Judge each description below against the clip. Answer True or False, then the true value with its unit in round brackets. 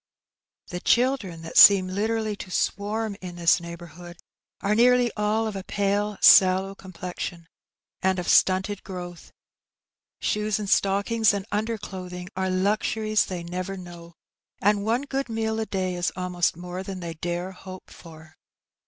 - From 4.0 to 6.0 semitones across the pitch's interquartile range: False (3.0 semitones)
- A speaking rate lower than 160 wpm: True (150 wpm)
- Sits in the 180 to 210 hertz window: True (190 Hz)